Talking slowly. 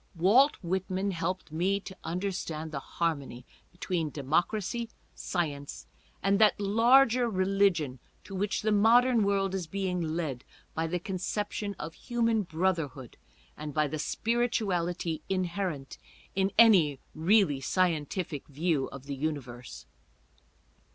Yes: slow, 120 wpm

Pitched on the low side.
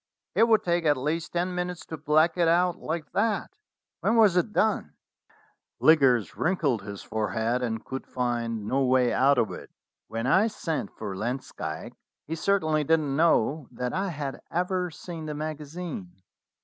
No: medium, 155 Hz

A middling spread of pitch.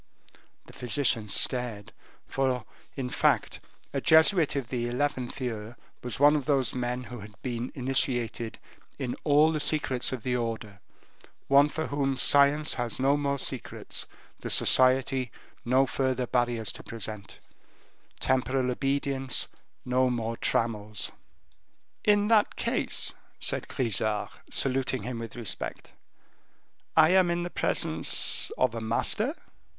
Yes: average, 3.0 semitones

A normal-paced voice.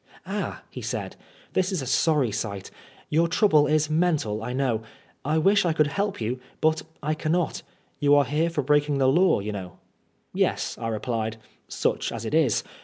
Yes: average, 180 wpm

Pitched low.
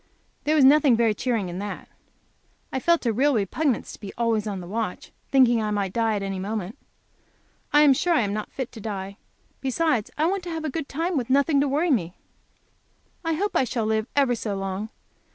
No: high, 235 Hz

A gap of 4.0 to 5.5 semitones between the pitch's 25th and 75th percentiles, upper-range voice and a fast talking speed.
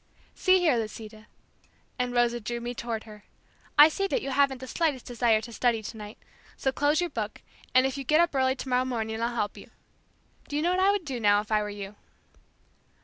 Yes: average, 4.5 semitones; high, 245 Hz; fast, 215 wpm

